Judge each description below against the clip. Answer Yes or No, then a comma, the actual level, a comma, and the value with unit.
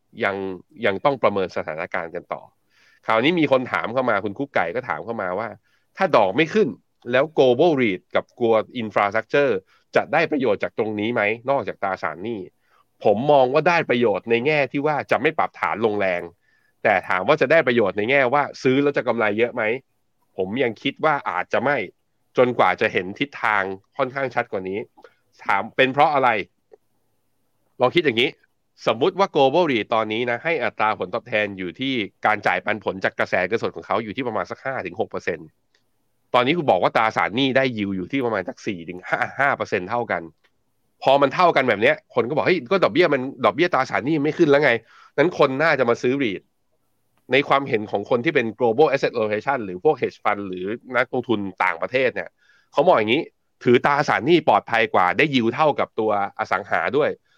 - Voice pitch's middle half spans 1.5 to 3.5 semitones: No, average, 4.6 semitones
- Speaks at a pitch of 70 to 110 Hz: No, low, 120 Hz